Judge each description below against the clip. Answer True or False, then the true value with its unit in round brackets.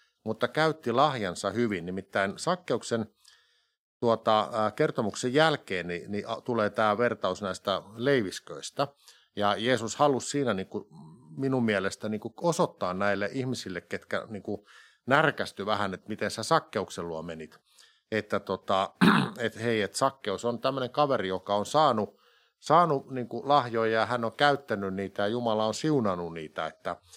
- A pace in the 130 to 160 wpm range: True (145 wpm)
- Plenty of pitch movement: False (4.5 semitones)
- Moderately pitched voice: False (110 Hz)